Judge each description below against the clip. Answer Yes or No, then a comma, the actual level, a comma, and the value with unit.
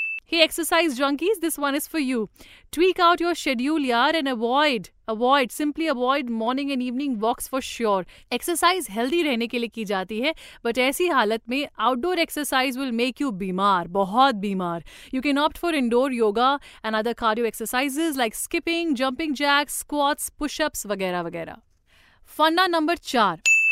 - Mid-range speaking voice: No, very high, 270 Hz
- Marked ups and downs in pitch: No, average, 5.0 semitones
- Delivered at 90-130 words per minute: No, average, 140 wpm